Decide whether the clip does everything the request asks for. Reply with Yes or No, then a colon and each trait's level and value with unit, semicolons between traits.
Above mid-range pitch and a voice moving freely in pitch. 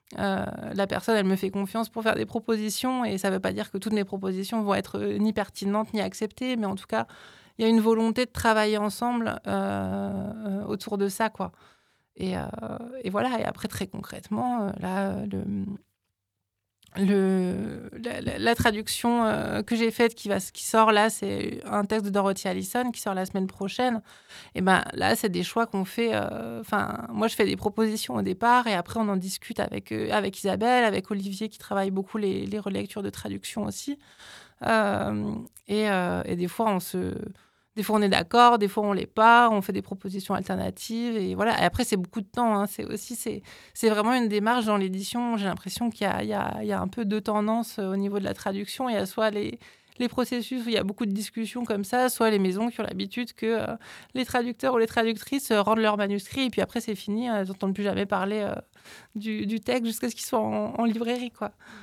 No: high, 210 Hz; average, 2.8 semitones